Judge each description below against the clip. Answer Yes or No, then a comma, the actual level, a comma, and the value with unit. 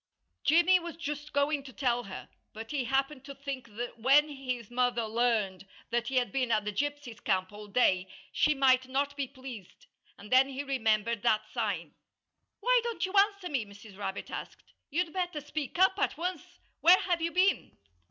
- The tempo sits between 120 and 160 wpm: No, average, 185 wpm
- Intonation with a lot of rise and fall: No, average, 4.7 semitones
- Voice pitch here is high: Yes, very high, 270 Hz